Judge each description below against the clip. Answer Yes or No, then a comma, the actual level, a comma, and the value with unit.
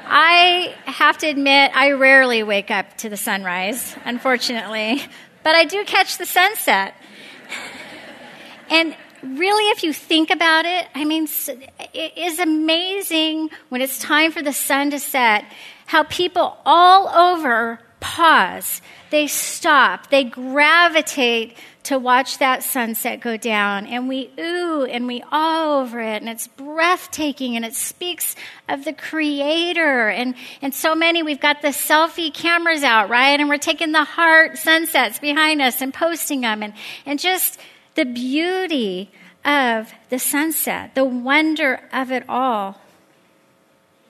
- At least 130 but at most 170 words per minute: Yes, average, 145 wpm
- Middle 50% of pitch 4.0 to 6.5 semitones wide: Yes, average, 4.6 semitones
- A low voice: No, very high, 290 Hz